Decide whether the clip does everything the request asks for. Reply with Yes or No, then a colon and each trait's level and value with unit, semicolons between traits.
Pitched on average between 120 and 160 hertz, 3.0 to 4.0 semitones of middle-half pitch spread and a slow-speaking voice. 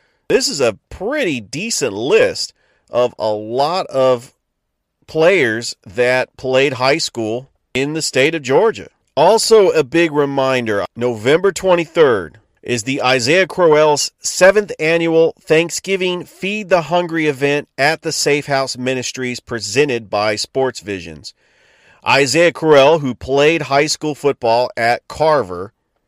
No: medium, 140 Hz; average, 5.2 semitones; slow, 125 wpm